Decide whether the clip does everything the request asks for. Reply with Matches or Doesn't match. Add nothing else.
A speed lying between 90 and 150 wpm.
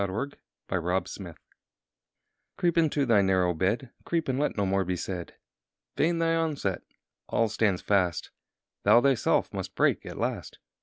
Doesn't match